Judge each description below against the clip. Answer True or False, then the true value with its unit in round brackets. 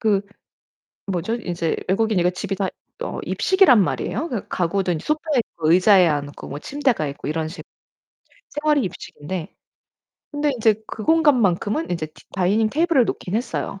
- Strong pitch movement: True (7.3 semitones)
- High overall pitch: True (205 Hz)